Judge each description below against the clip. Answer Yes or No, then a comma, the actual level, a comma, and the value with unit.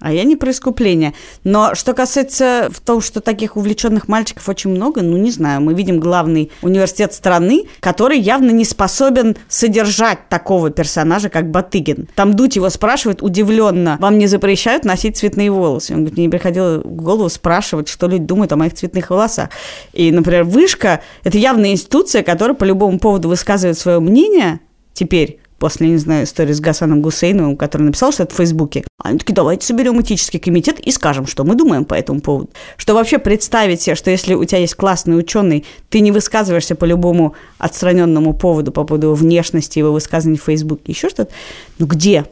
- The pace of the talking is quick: Yes, fast, 180 wpm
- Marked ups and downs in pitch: No, average, 4.6 semitones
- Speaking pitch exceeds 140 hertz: Yes, medium, 185 Hz